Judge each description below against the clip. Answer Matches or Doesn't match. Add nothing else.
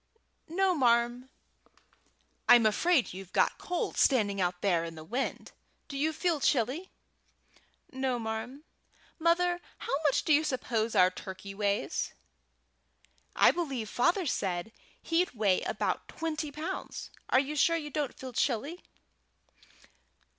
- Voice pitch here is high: Matches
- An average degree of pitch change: Doesn't match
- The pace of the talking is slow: Matches